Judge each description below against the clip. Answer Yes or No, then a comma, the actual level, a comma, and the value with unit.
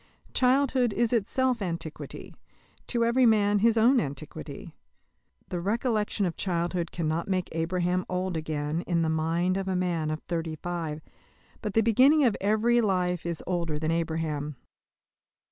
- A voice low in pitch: No, medium, 180 Hz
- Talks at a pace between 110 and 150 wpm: Yes, average, 145 wpm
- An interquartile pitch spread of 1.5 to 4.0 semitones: No, average, 5.1 semitones